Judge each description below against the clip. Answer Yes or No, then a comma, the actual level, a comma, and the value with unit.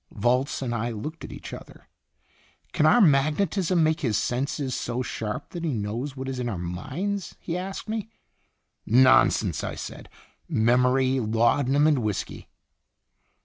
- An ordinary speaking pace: Yes, average, 145 wpm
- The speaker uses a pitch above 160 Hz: No, low, 130 Hz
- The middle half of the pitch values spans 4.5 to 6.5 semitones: Yes, average, 5.0 semitones